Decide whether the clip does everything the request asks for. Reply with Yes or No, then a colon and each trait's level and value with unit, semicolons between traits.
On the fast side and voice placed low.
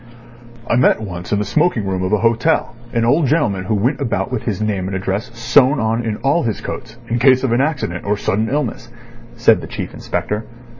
Yes: fast, 215 wpm; low, 115 Hz